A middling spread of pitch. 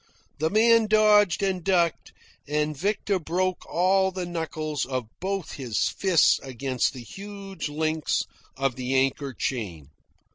No: wide, 6.2 semitones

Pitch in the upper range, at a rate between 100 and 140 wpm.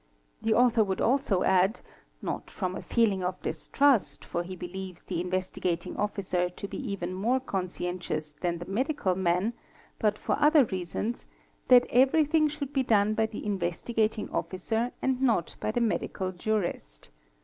No: high, 200 Hz; average, 160 wpm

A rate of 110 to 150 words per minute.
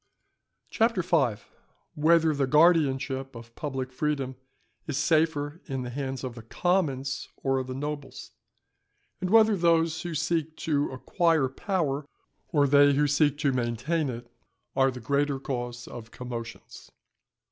Yes: slow, 135 wpm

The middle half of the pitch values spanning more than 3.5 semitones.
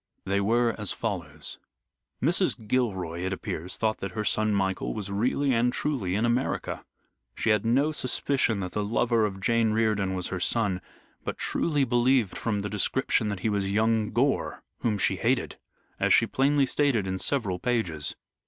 Yes: average, 3.9 semitones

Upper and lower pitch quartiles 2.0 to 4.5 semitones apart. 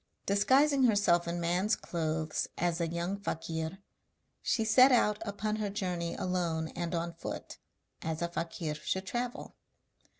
Yes: average, 3.9 semitones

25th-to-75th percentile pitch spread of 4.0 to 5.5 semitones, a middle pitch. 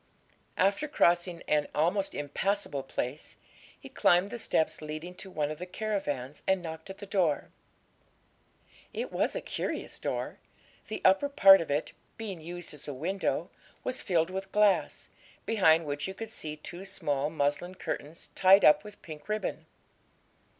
Yes: average, 4.4 semitones; medium, 175 Hz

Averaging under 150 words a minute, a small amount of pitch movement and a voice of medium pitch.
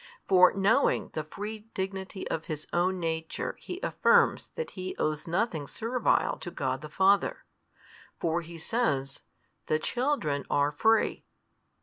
No: slow, 135 wpm; average, 5.3 semitones; medium, 180 Hz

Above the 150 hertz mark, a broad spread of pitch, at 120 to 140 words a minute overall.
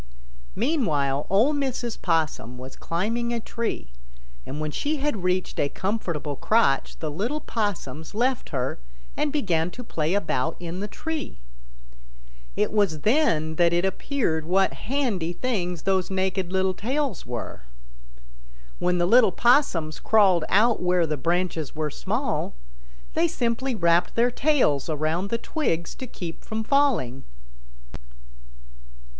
Yes: medium, 185 Hz; wide, 6.7 semitones; slow, 135 wpm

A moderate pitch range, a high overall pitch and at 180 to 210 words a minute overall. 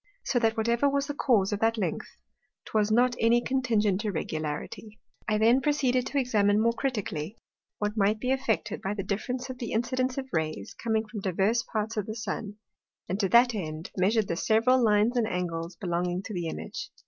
Yes: average, 3.7 semitones; high, 220 Hz; average, 190 wpm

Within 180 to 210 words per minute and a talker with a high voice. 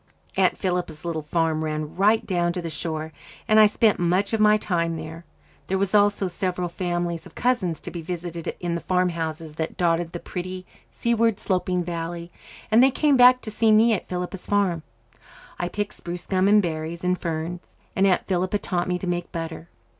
No: average, 190 wpm; medium, 180 Hz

